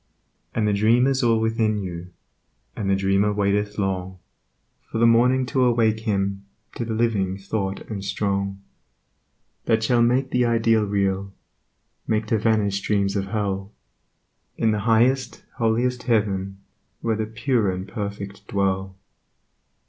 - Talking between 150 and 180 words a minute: No, average, 140 wpm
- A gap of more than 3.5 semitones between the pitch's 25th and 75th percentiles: No, average, 2.7 semitones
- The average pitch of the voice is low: Yes, low, 105 Hz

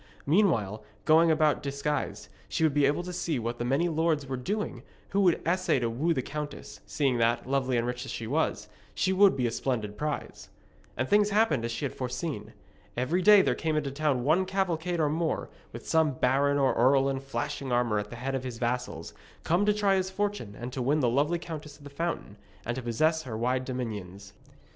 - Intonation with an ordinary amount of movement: Yes, average, 5.0 semitones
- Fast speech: Yes, fast, 215 wpm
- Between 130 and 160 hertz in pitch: Yes, medium, 140 Hz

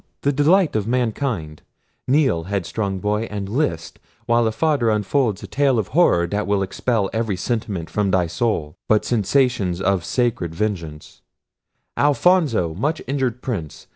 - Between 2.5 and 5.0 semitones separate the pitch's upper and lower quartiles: No, wide, 5.4 semitones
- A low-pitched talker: Yes, low, 110 Hz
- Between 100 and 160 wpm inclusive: Yes, average, 140 wpm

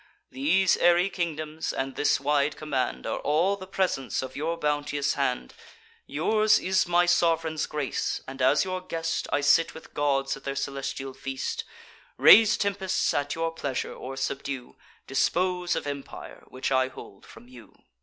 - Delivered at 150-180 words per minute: Yes, average, 155 wpm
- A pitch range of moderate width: Yes, average, 4.4 semitones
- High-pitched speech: No, medium, 150 Hz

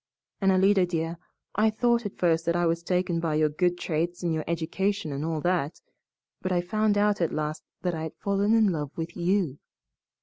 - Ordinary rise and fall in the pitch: Yes, average, 3.3 semitones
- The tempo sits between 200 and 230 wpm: Yes, fast, 205 wpm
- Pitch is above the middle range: No, medium, 175 Hz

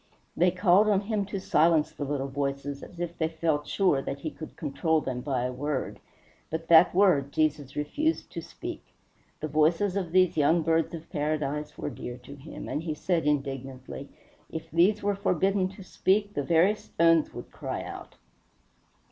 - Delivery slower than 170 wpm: No, average, 180 wpm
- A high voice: No, medium, 160 Hz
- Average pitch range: Yes, average, 4.1 semitones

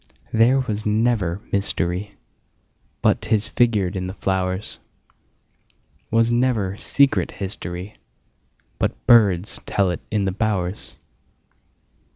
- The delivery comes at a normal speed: No, slow, 90 wpm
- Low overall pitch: Yes, low, 105 Hz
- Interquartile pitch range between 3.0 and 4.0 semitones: Yes, average, 3.5 semitones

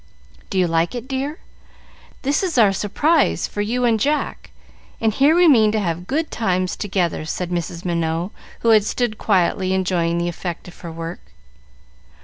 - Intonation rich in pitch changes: Yes, wide, 5.9 semitones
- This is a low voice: No, high, 195 Hz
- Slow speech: No, average, 170 wpm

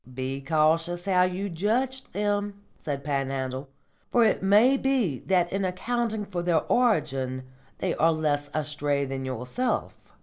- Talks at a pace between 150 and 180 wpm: No, average, 140 wpm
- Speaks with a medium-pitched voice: Yes, medium, 175 Hz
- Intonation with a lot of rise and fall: Yes, wide, 6.6 semitones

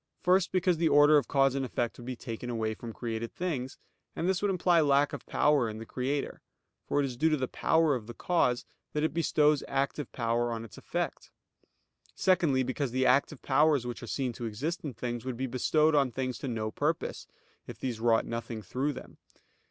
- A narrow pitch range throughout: No, average, 4.1 semitones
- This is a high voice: No, low, 130 Hz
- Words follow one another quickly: Yes, fast, 210 wpm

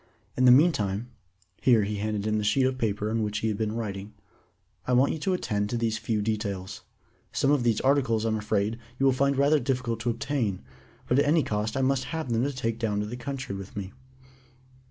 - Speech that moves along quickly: Yes, fast, 220 wpm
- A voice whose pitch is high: No, low, 115 Hz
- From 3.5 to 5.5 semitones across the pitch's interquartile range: Yes, average, 3.8 semitones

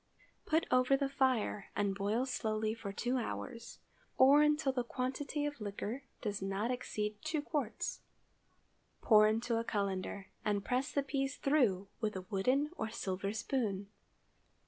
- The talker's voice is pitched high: Yes, high, 230 Hz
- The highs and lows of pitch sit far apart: No, average, 4.7 semitones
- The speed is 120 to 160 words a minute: Yes, average, 150 wpm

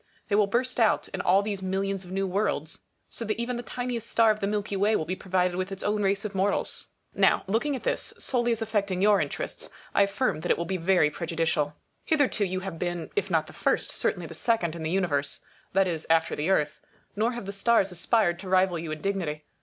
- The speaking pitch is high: Yes, high, 195 Hz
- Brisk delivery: Yes, fast, 235 wpm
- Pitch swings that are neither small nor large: Yes, average, 3.4 semitones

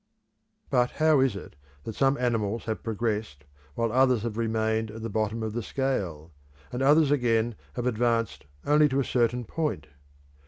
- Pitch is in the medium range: No, low, 115 Hz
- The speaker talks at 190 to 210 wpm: No, average, 165 wpm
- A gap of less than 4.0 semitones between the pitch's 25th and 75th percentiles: Yes, average, 3.0 semitones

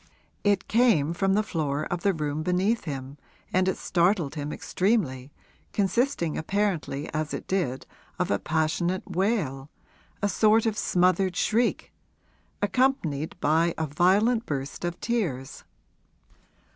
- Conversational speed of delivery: No, slow, 130 wpm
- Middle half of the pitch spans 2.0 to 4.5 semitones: No, average, 5.2 semitones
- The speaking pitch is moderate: Yes, medium, 175 Hz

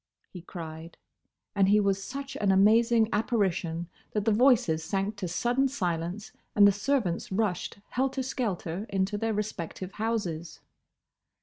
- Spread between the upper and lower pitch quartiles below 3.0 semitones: No, average, 4.0 semitones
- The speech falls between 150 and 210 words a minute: No, slow, 135 wpm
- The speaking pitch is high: Yes, high, 200 Hz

